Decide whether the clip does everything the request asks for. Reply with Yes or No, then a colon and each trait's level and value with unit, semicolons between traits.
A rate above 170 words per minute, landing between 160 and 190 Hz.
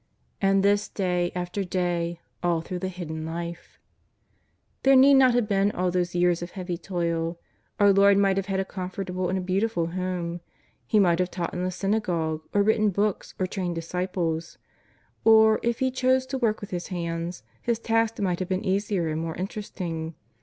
Yes: average, 185 wpm; medium, 185 Hz